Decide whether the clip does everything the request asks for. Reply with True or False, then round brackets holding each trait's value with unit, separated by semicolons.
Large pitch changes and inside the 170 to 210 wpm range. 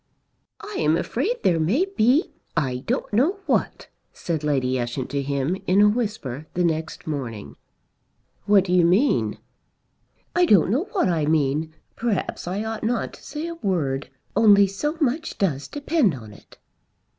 False (8.5 semitones; 160 wpm)